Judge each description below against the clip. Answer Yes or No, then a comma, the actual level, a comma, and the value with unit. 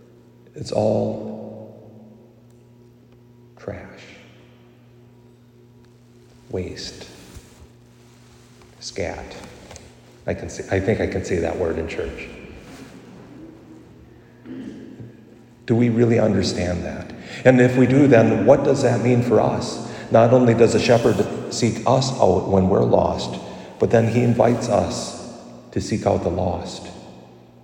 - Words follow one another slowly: Yes, slow, 115 wpm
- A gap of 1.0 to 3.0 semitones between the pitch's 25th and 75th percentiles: No, average, 4.2 semitones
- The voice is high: No, low, 115 Hz